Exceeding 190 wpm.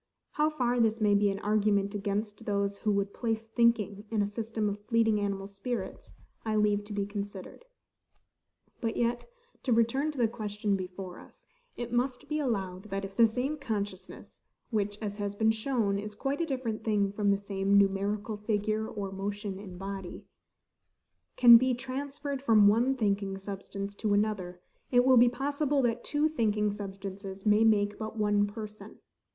No: average, 170 wpm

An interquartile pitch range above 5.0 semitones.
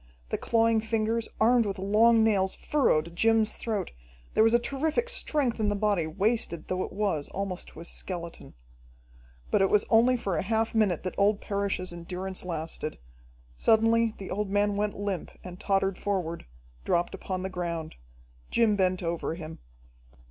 No: average, 3.5 semitones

